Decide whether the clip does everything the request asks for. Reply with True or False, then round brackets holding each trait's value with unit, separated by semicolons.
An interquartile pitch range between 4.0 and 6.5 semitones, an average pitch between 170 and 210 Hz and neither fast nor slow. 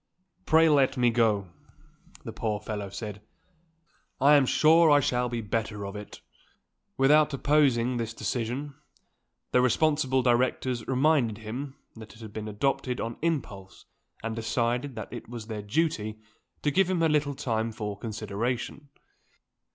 False (4.5 semitones; 120 Hz; 150 wpm)